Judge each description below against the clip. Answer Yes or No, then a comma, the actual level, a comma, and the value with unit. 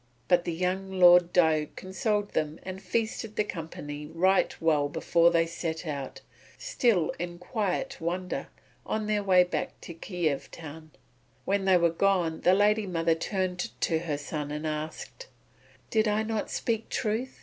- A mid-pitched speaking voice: Yes, medium, 180 Hz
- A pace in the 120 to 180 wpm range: Yes, average, 160 wpm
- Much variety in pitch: No, average, 3.8 semitones